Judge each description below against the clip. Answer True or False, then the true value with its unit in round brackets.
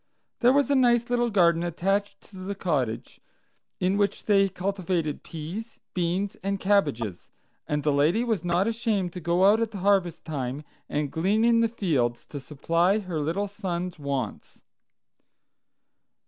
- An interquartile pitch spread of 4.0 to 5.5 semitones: True (4.4 semitones)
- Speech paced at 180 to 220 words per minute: False (150 wpm)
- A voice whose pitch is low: False (185 Hz)